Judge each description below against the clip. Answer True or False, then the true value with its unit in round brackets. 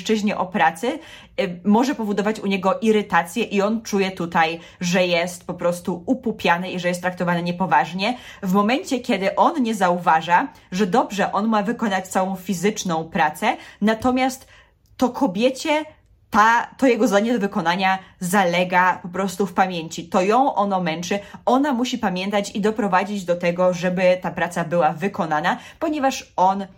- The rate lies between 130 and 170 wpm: True (150 wpm)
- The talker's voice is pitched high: True (195 Hz)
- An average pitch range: True (3.7 semitones)